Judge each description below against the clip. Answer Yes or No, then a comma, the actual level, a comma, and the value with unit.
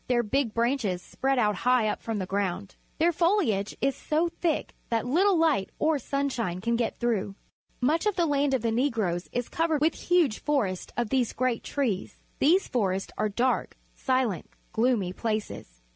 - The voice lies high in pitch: Yes, high, 245 Hz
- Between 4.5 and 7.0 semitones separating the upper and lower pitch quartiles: Yes, wide, 5.5 semitones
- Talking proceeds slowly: No, average, 175 wpm